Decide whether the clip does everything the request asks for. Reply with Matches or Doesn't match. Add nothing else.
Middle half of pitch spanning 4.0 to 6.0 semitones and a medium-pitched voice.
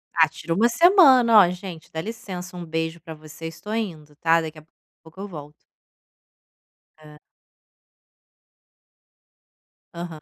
Matches